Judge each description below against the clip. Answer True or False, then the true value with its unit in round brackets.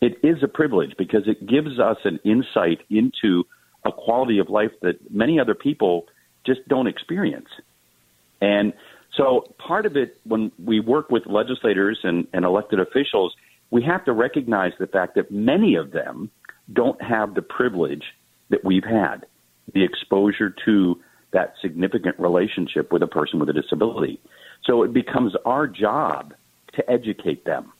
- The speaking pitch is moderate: False (100 Hz)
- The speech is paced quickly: False (160 wpm)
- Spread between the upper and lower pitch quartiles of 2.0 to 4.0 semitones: False (4.4 semitones)